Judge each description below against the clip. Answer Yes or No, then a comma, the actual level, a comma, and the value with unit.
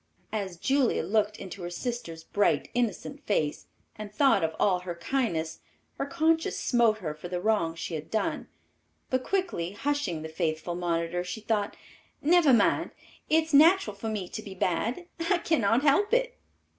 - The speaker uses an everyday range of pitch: No, wide, 7.9 semitones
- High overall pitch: Yes, high, 210 Hz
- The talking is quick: No, average, 170 wpm